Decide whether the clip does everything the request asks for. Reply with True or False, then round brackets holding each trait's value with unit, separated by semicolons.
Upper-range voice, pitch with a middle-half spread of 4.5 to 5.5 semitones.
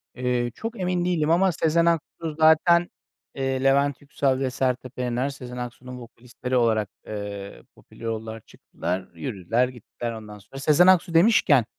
False (130 Hz; 5.2 semitones)